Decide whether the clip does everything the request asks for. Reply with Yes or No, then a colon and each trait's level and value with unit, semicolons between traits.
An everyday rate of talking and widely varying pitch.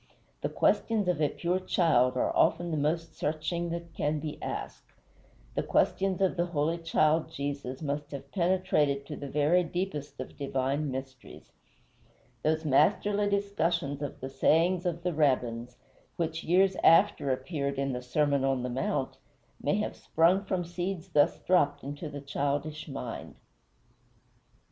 No: average, 150 wpm; average, 3.8 semitones